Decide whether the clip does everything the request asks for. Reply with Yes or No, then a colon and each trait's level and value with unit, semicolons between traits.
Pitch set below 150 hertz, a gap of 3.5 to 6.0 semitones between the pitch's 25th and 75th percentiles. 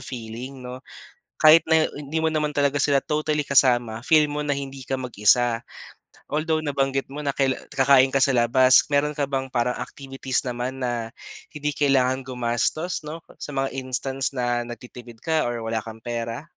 No: low, 135 Hz; average, 3.1 semitones